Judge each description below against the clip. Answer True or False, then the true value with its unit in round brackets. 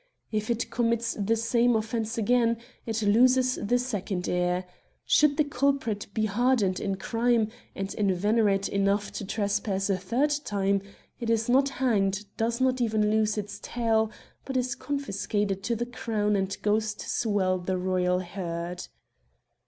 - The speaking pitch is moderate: False (215 Hz)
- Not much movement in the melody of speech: False (3.2 semitones)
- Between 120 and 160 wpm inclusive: True (155 wpm)